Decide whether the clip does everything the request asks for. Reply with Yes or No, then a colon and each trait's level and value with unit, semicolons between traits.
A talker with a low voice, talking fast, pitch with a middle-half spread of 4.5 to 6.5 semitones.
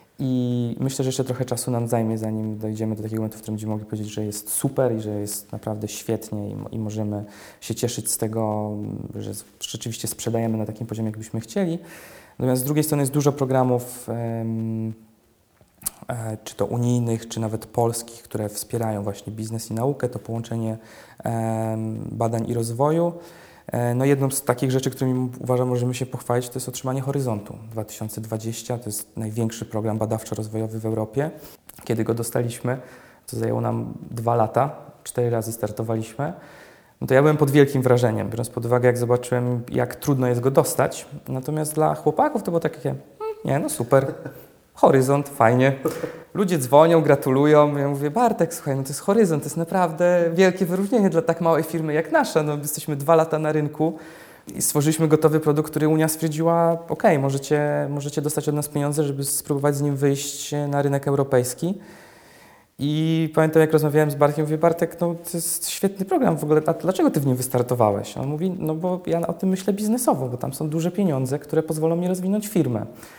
Yes: low, 130 Hz; fast, 180 wpm; wide, 5.5 semitones